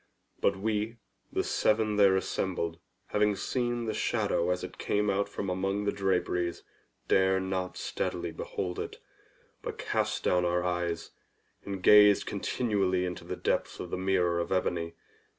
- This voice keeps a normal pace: Yes, average, 150 wpm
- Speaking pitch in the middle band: No, very low, 95 Hz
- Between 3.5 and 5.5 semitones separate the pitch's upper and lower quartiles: No, narrow, 2.5 semitones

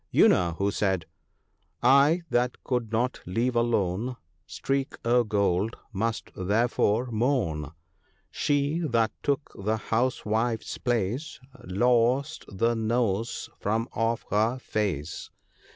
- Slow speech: Yes, slow, 125 wpm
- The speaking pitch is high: No, low, 115 Hz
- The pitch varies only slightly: No, average, 3.5 semitones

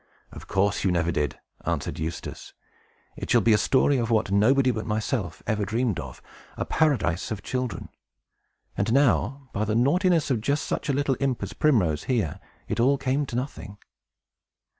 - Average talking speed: Yes, average, 175 wpm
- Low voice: Yes, low, 115 Hz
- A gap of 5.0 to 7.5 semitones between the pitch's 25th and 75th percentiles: Yes, average, 5.3 semitones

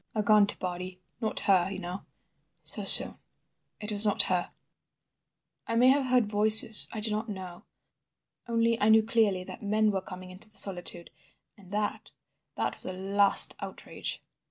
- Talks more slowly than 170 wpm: Yes, average, 160 wpm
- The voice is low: No, high, 205 Hz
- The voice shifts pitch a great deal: No, average, 2.7 semitones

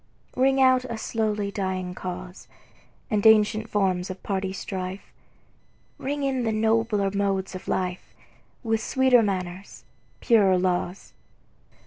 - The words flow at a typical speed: No, slow, 120 wpm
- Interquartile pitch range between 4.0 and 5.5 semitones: No, average, 3.2 semitones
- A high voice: Yes, high, 200 Hz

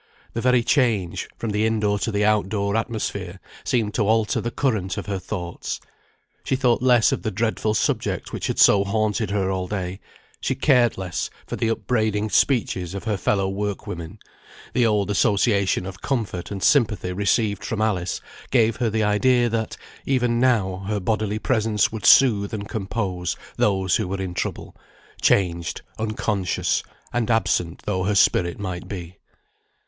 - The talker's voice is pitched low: Yes, low, 105 Hz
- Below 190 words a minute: Yes, average, 170 wpm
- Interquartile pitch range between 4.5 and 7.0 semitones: No, average, 2.8 semitones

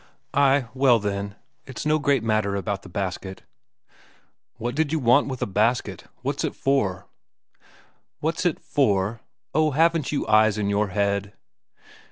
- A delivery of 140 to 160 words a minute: Yes, average, 150 wpm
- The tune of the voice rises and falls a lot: Yes, wide, 5.8 semitones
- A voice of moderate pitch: No, low, 115 Hz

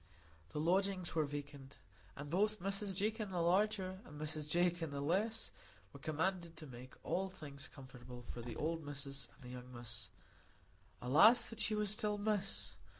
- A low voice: No, medium, 165 Hz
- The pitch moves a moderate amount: No, wide, 5.8 semitones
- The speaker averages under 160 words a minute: No, average, 165 wpm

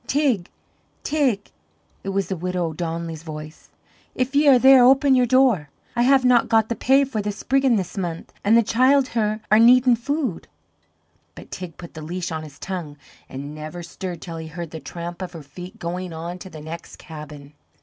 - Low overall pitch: No, medium, 185 Hz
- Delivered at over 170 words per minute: Yes, average, 190 wpm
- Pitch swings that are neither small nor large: No, wide, 7.1 semitones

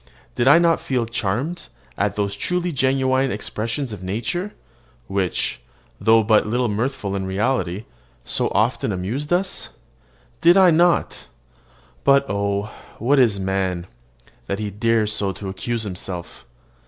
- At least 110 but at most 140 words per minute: Yes, slow, 135 wpm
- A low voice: Yes, low, 110 Hz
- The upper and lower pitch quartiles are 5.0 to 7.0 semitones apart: Yes, wide, 5.4 semitones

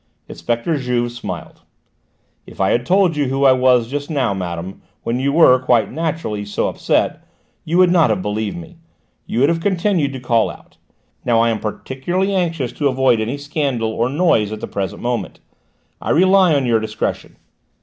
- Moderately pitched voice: No, low, 130 Hz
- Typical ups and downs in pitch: No, wide, 6.0 semitones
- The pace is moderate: Yes, average, 180 wpm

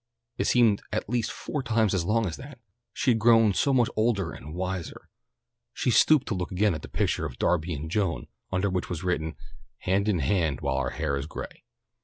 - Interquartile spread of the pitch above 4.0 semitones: Yes, average, 5.2 semitones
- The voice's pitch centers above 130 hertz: No, very low, 95 Hz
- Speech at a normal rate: No, fast, 210 wpm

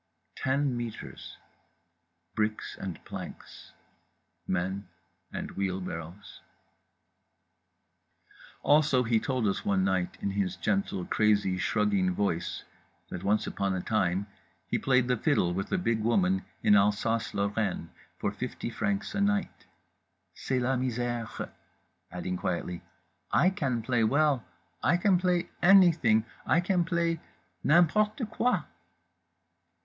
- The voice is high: No, low, 110 Hz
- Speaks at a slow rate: Yes, slow, 115 wpm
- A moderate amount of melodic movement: No, wide, 7.2 semitones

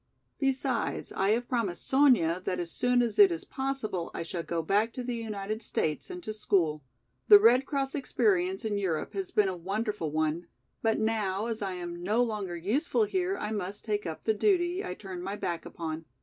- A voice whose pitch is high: Yes, high, 210 Hz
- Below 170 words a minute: No, average, 200 wpm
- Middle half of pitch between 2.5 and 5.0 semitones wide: No, wide, 5.6 semitones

